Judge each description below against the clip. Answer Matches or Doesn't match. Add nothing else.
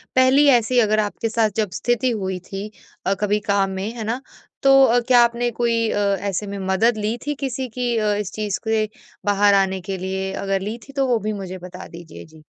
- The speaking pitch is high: Matches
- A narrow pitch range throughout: Doesn't match